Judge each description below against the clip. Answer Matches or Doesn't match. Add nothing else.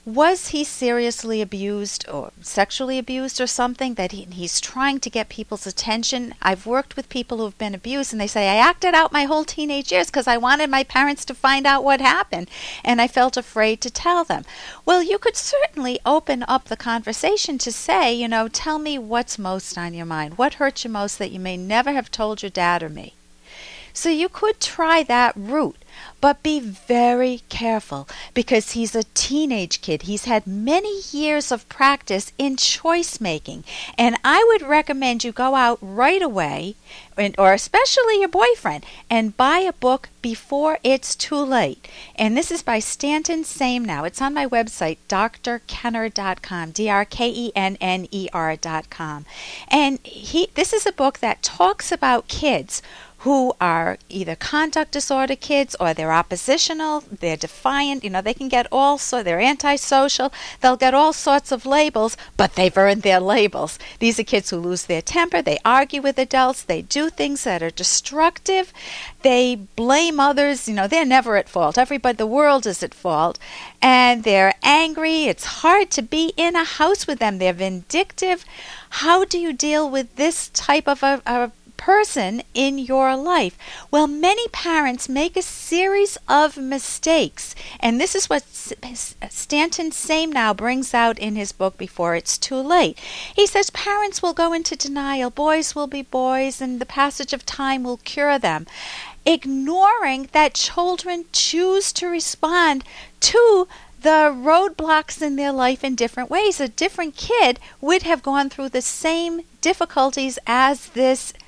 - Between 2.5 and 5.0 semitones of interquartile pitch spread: Doesn't match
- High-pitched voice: Matches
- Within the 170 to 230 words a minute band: Matches